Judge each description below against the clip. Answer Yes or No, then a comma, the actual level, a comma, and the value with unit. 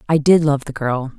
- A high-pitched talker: No, medium, 145 Hz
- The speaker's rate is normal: No, fast, 255 wpm